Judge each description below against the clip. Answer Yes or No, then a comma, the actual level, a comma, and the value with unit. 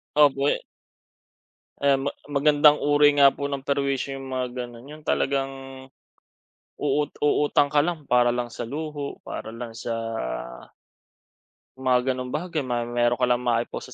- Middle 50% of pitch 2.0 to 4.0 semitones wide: Yes, average, 2.8 semitones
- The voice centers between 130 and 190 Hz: Yes, low, 135 Hz